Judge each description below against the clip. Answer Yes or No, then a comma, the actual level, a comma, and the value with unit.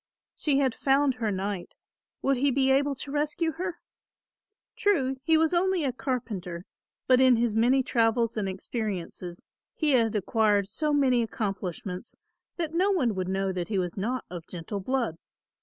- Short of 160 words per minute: No, average, 165 wpm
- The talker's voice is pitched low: No, high, 240 Hz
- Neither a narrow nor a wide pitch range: No, wide, 6.0 semitones